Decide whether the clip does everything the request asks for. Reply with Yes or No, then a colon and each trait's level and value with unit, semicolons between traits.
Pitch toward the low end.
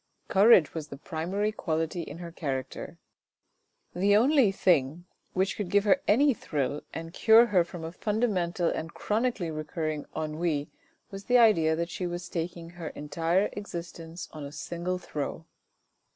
No: medium, 170 Hz